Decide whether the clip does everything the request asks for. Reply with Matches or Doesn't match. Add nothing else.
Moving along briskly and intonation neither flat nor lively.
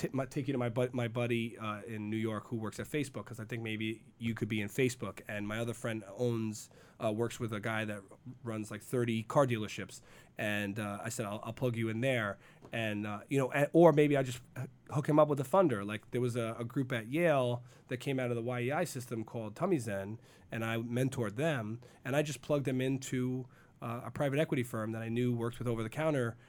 Matches